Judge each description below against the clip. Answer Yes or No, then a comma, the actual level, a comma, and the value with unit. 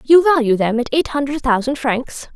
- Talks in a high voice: Yes, very high, 265 Hz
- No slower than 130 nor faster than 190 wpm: No, fast, 205 wpm